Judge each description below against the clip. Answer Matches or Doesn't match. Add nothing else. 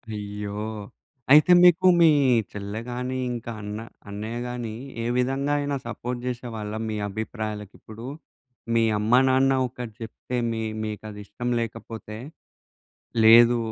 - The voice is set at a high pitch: Doesn't match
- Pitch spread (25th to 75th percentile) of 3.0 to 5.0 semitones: Doesn't match